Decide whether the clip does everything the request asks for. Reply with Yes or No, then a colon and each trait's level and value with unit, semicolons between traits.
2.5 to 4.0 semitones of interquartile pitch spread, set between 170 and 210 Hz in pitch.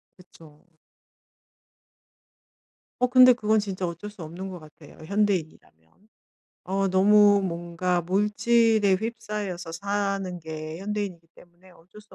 Yes: average, 3.3 semitones; high, 190 Hz